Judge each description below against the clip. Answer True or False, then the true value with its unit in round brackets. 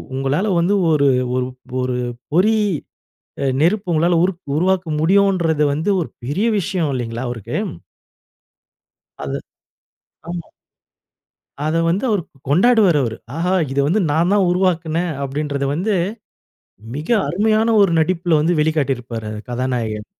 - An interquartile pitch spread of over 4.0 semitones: True (5.1 semitones)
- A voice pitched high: False (165 Hz)